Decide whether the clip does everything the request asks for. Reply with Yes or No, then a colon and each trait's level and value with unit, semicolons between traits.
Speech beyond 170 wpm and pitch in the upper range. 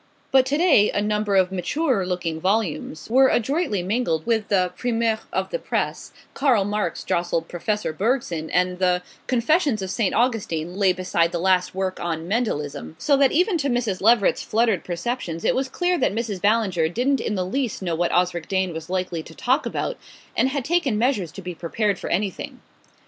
Yes: average, 185 wpm; high, 200 Hz